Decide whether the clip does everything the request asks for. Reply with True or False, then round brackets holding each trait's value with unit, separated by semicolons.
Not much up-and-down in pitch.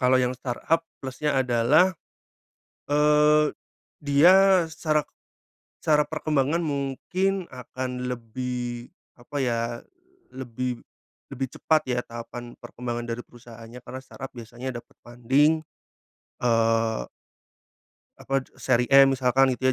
False (3.7 semitones)